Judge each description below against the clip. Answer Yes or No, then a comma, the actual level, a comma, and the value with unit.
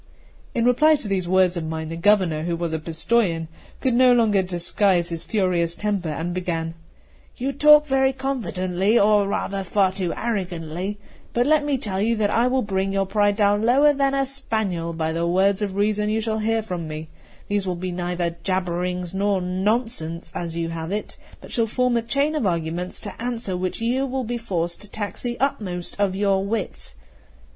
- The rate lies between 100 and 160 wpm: No, average, 195 wpm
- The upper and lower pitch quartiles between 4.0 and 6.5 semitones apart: Yes, average, 4.7 semitones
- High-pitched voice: Yes, high, 195 Hz